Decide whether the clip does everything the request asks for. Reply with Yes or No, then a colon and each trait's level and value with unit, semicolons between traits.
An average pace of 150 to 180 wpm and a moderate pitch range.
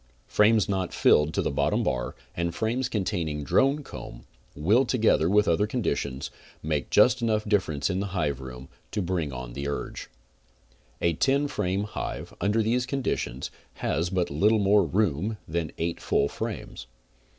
No: average, 155 wpm; wide, 6.1 semitones